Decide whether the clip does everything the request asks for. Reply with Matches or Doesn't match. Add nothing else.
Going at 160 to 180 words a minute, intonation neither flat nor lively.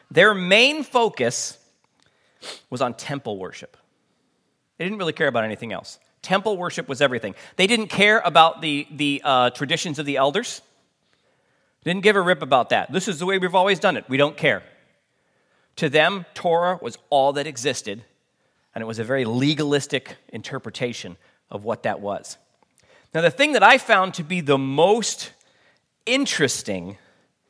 Doesn't match